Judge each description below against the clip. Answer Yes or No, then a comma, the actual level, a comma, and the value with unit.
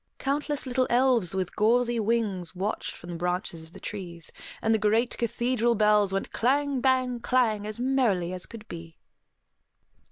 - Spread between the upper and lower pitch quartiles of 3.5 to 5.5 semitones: Yes, average, 4.9 semitones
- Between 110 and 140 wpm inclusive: No, average, 160 wpm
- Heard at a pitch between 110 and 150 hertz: No, high, 220 Hz